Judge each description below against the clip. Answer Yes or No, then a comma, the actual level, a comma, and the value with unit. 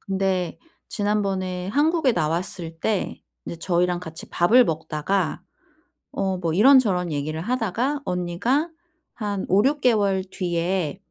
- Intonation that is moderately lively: Yes, average, 3.8 semitones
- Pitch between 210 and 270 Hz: No, high, 190 Hz